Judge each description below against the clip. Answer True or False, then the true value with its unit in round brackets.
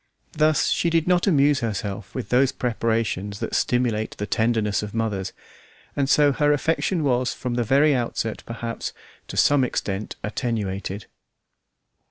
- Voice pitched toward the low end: True (120 Hz)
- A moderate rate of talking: True (145 wpm)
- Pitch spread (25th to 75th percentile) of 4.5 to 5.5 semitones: True (5.0 semitones)